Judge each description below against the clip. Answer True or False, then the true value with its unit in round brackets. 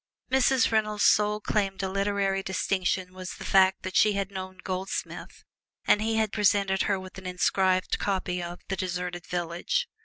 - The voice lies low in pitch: False (190 Hz)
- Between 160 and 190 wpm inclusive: True (165 wpm)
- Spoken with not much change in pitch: True (1.8 semitones)